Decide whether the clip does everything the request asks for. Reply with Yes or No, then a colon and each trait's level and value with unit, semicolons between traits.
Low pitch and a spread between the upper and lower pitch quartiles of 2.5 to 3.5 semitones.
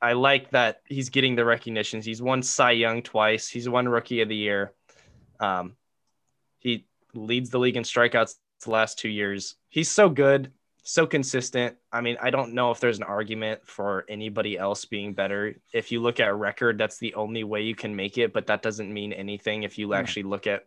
Yes: low, 115 Hz; average, 2.8 semitones